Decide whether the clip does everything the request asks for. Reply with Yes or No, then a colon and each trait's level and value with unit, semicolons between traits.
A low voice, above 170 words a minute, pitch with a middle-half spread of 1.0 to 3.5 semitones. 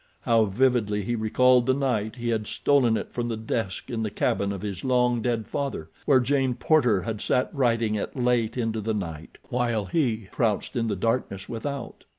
Yes: low, 115 Hz; average, 190 wpm; average, 2.9 semitones